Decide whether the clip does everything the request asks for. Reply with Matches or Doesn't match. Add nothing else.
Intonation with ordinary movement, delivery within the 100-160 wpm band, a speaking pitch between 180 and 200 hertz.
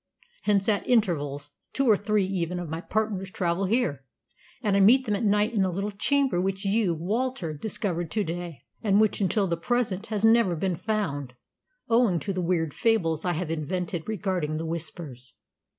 Doesn't match